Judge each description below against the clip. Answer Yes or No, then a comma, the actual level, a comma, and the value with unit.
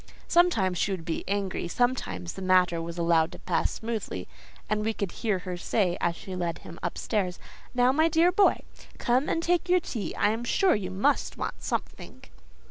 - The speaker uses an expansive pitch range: Yes, wide, 5.9 semitones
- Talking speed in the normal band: Yes, average, 190 wpm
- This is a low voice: No, high, 200 Hz